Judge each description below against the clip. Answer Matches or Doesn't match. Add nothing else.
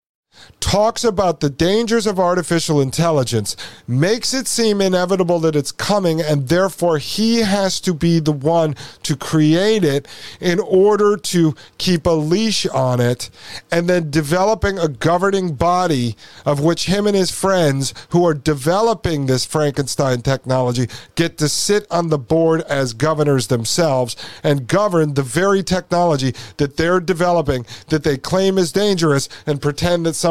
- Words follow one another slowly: Doesn't match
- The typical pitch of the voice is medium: Matches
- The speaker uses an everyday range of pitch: Matches